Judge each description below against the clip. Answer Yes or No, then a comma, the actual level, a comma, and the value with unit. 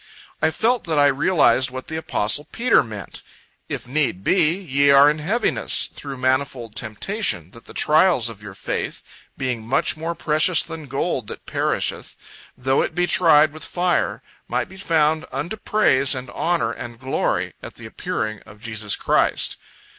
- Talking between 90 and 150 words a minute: No, average, 165 wpm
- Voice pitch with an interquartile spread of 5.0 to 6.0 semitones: Yes, wide, 5.4 semitones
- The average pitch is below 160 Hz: Yes, medium, 140 Hz